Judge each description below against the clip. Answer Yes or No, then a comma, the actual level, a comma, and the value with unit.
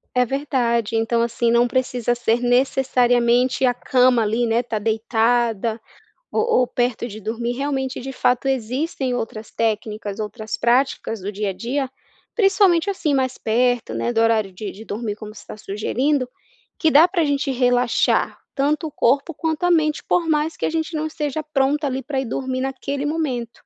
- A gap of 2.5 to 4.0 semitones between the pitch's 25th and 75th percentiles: Yes, average, 3.6 semitones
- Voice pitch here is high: Yes, very high, 250 Hz